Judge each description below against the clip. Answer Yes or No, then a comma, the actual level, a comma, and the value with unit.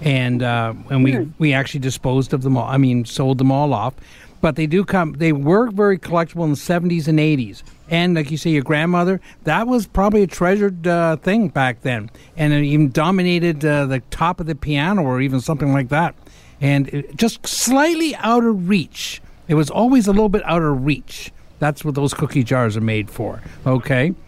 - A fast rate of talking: Yes, fast, 210 wpm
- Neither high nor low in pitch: Yes, medium, 150 Hz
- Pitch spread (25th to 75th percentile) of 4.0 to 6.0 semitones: Yes, average, 4.7 semitones